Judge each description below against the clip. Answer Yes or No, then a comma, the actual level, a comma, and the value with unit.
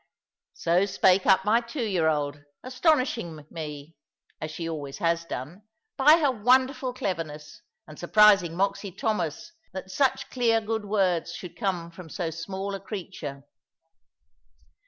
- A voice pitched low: No, high, 190 Hz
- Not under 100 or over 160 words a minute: Yes, slow, 135 wpm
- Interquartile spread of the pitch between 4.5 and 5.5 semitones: Yes, average, 4.9 semitones